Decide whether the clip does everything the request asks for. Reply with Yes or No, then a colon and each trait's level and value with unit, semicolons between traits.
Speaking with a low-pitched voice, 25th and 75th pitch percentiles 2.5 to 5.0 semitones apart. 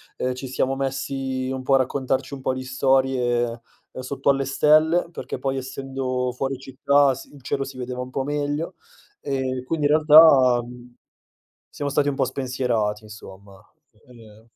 No: low, 130 Hz; narrow, 1.5 semitones